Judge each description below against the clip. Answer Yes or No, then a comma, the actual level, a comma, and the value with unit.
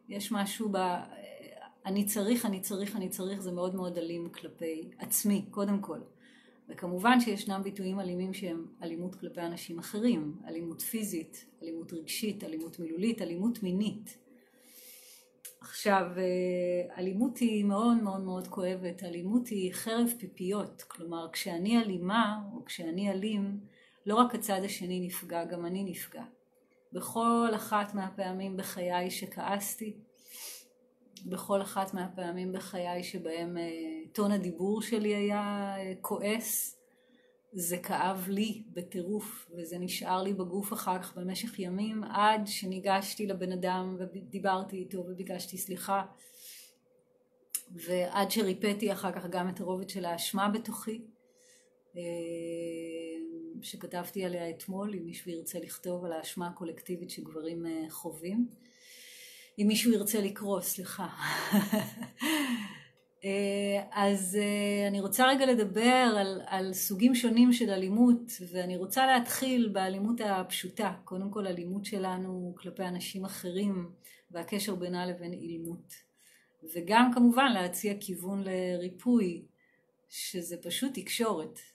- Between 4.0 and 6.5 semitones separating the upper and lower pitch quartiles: No, average, 3.3 semitones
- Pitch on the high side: Yes, high, 195 Hz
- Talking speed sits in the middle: Yes, average, 115 wpm